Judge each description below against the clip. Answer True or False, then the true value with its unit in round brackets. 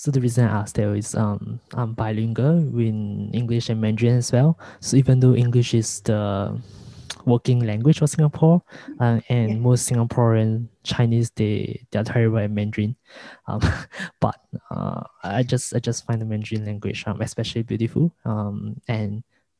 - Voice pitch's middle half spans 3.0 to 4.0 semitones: False (2.5 semitones)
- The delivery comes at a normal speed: True (155 wpm)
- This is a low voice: True (115 Hz)